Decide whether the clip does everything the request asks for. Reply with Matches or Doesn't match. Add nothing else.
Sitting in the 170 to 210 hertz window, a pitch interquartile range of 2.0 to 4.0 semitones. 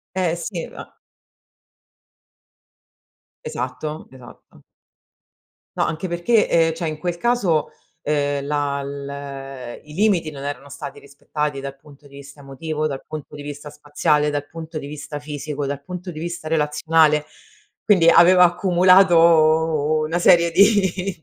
Doesn't match